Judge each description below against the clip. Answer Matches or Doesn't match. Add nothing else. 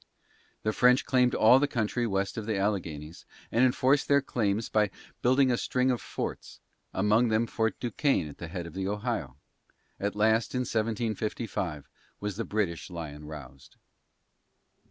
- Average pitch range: Matches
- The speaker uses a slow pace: Doesn't match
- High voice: Doesn't match